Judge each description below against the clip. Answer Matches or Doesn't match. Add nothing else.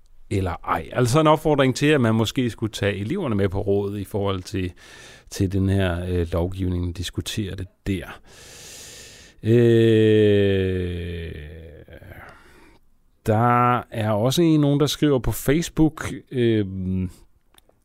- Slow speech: Matches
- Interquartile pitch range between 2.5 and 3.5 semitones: Doesn't match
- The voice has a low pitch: Matches